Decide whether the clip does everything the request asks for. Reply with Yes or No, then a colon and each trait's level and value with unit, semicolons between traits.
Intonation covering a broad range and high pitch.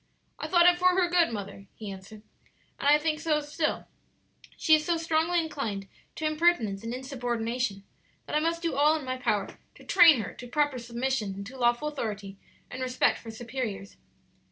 Yes: wide, 5.9 semitones; very high, 260 Hz